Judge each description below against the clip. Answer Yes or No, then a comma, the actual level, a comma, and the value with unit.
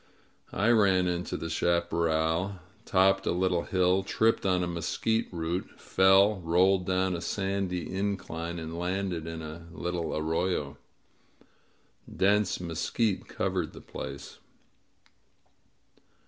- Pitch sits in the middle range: No, very low, 90 Hz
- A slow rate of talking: Yes, slow, 120 wpm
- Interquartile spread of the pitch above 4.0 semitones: No, narrow, 2.5 semitones